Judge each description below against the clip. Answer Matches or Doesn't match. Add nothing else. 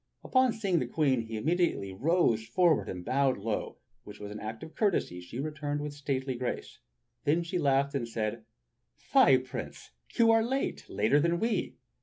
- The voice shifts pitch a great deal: Matches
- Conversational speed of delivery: Matches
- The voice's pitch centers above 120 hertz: Matches